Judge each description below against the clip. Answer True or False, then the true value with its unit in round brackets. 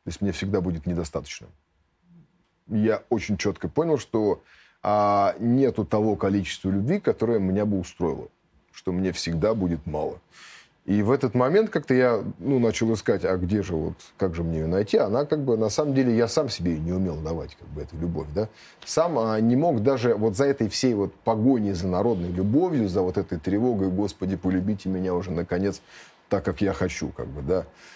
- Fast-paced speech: True (195 wpm)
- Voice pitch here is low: True (100 Hz)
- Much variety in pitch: False (4.2 semitones)